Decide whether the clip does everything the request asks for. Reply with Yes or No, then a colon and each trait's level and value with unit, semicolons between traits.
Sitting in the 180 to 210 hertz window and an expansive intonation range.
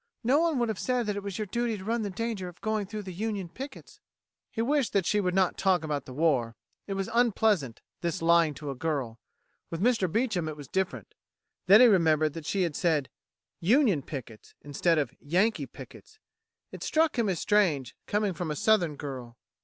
Yes: high, 190 Hz; wide, 5.9 semitones